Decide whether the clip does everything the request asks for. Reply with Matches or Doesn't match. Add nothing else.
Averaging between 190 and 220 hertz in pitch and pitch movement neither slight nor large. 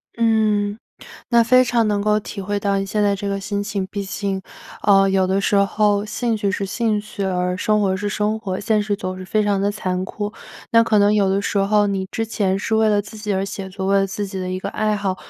Doesn't match